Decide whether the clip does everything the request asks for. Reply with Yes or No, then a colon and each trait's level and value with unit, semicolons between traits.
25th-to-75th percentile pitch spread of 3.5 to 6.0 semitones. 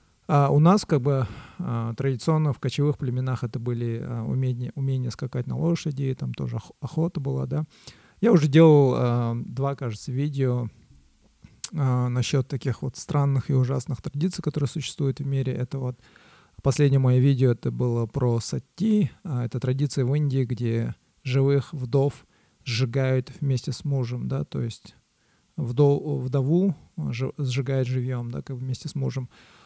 No: narrow, 2.4 semitones